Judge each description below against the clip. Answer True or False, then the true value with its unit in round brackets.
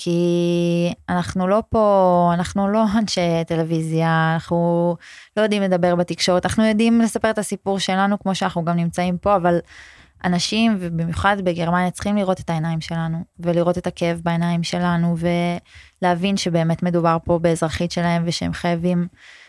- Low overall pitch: False (175 Hz)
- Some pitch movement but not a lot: False (2.1 semitones)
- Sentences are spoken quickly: False (140 wpm)